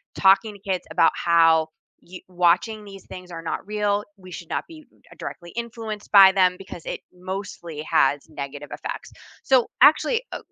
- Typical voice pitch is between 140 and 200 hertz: Yes, medium, 185 Hz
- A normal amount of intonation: Yes, average, 3.5 semitones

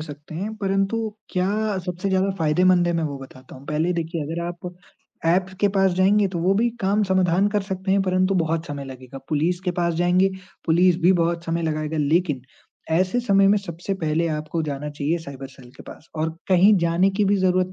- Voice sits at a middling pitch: Yes, medium, 175 Hz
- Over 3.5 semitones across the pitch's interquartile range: No, average, 3.2 semitones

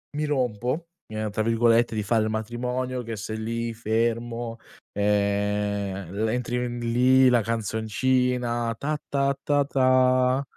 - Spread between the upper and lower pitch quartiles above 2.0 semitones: Yes, narrow, 2.6 semitones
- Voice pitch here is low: Yes, low, 115 Hz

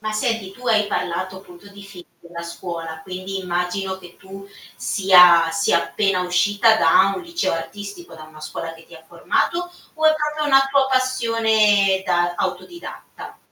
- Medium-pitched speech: No, high, 195 Hz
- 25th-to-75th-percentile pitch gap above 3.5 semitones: Yes, average, 4.4 semitones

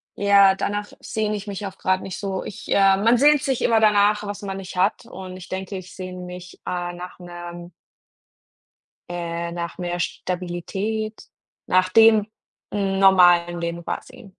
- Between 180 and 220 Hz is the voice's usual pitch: Yes, high, 190 Hz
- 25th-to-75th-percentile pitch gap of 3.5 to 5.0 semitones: No, average, 2.7 semitones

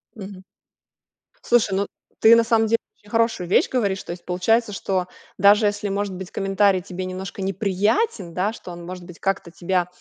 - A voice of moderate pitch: No, high, 195 Hz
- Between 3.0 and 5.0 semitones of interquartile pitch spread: No, narrow, 2.4 semitones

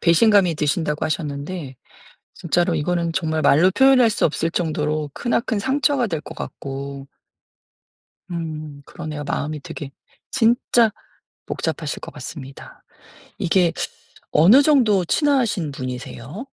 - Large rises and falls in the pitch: Yes, wide, 6.3 semitones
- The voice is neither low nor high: Yes, medium, 165 Hz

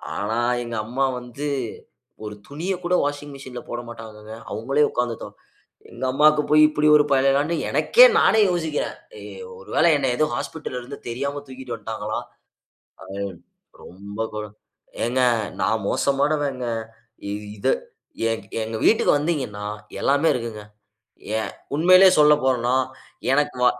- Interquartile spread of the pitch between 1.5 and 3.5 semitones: No, average, 4.2 semitones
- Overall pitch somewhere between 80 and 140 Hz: Yes, low, 135 Hz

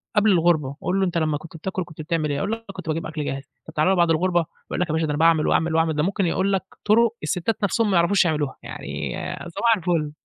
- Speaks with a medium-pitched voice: Yes, medium, 170 Hz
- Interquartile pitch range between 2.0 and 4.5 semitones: Yes, average, 3.5 semitones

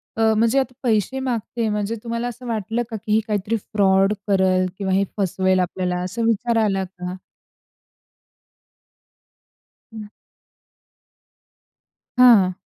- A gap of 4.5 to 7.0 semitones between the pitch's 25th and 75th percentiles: No, average, 3.4 semitones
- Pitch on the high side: Yes, high, 210 Hz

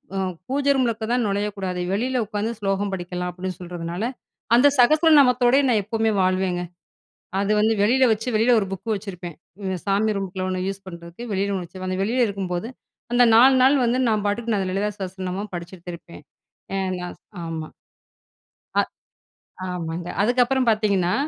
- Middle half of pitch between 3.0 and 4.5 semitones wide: Yes, average, 4.1 semitones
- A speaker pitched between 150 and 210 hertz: Yes, high, 200 Hz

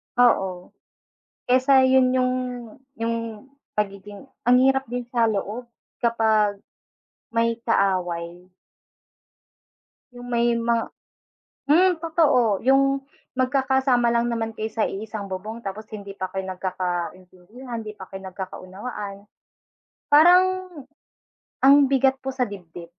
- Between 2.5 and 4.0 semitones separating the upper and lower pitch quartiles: No, average, 4.6 semitones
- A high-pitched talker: Yes, high, 230 Hz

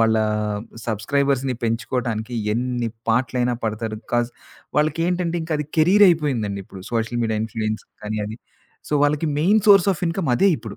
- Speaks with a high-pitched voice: No, low, 125 Hz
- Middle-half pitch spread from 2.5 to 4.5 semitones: No, wide, 5.6 semitones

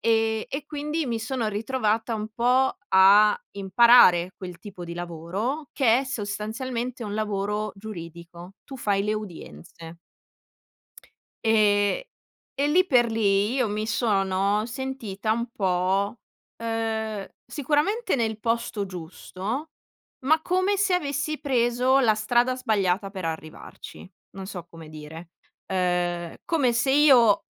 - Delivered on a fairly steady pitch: No, average, 4.7 semitones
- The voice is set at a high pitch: Yes, high, 215 Hz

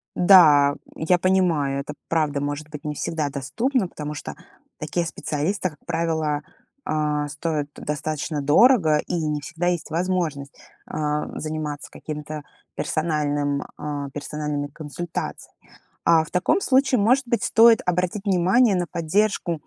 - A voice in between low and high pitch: Yes, medium, 155 Hz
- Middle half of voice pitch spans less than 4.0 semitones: Yes, average, 3.4 semitones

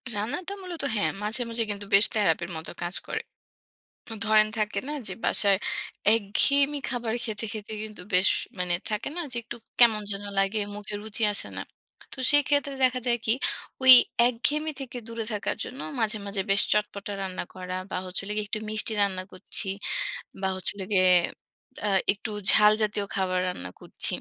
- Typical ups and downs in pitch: Yes, average, 3.1 semitones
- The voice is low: No, high, 210 Hz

